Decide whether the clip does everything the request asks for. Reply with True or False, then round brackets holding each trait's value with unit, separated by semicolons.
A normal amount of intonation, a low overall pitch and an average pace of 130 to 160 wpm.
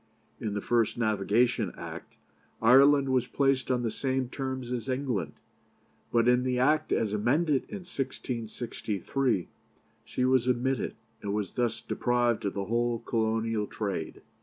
True (3.0 semitones; 120 Hz; 140 wpm)